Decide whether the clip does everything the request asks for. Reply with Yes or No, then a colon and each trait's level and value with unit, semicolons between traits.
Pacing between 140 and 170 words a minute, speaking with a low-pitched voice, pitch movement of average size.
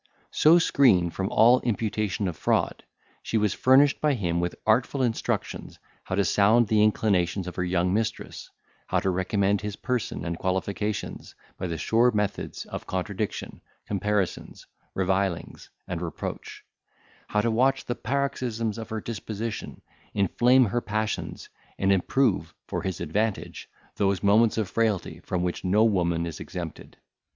Yes: average, 145 wpm; low, 105 Hz; average, 3.5 semitones